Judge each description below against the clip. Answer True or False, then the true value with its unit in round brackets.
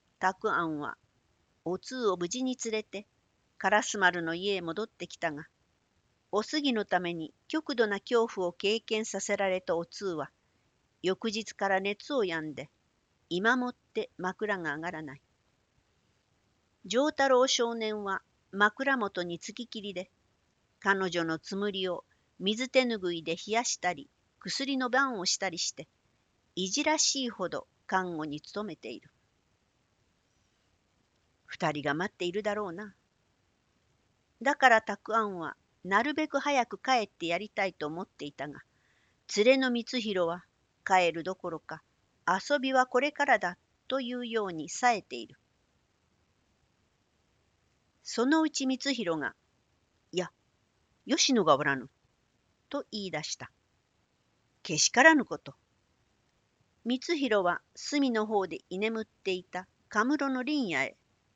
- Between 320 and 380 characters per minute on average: False (235 characters per minute)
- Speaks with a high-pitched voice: True (200 Hz)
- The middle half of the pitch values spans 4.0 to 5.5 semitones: False (6.5 semitones)